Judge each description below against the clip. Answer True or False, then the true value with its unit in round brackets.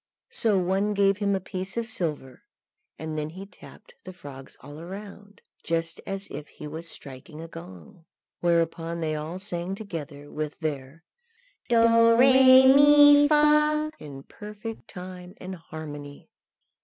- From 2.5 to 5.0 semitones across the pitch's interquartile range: False (5.5 semitones)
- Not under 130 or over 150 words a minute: True (145 wpm)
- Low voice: False (180 Hz)